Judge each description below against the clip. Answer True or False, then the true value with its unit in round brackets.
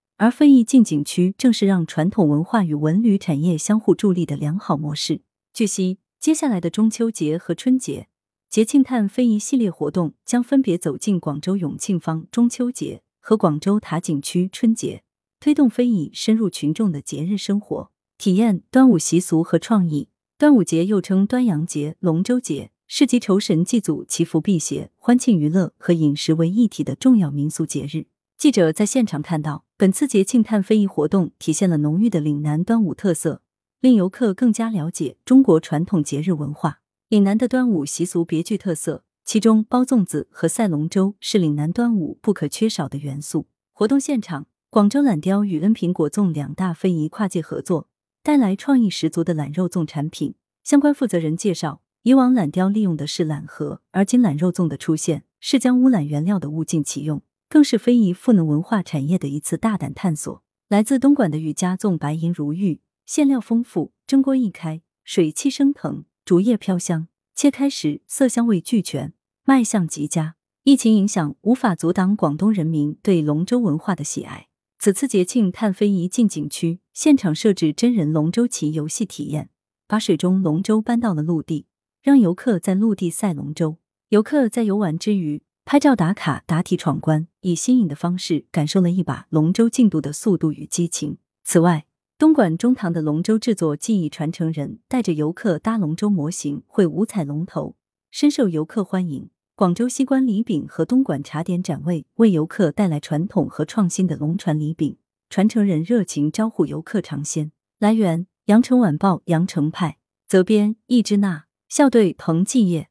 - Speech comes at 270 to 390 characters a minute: True (280 characters per minute)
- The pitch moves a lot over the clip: True (6.0 semitones)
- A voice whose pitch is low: False (185 Hz)